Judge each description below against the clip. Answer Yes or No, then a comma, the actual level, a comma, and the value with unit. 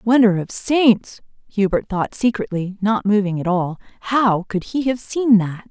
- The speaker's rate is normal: Yes, average, 170 wpm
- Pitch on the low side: No, high, 210 Hz